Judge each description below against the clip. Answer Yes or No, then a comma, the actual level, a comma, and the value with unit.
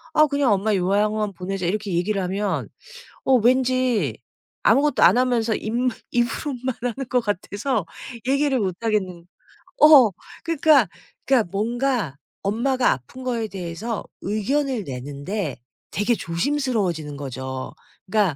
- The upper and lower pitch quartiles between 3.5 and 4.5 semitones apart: No, wide, 5.5 semitones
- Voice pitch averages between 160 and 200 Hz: No, high, 215 Hz